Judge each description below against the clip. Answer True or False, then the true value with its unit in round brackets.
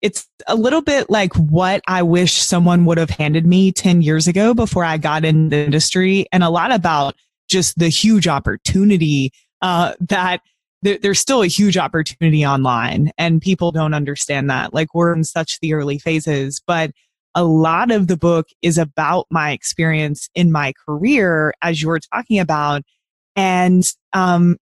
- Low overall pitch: False (170 Hz)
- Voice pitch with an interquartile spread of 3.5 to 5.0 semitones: False (3.1 semitones)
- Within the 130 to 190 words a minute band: True (170 wpm)